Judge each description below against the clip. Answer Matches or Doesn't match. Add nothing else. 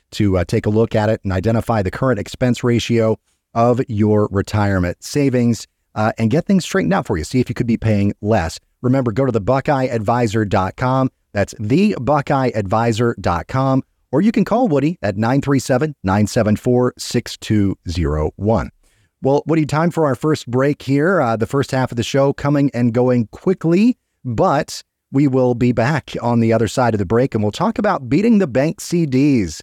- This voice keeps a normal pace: Matches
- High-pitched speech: Doesn't match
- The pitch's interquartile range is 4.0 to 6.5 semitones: Matches